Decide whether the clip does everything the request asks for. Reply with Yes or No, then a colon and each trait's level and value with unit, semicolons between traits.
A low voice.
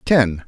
Yes: low, 115 Hz